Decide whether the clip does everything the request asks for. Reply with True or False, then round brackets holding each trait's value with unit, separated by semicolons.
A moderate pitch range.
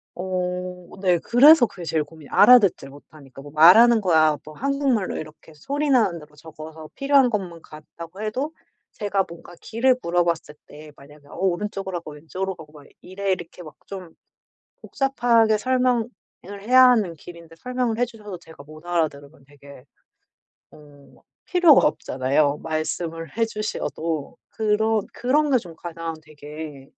False (6.3 semitones)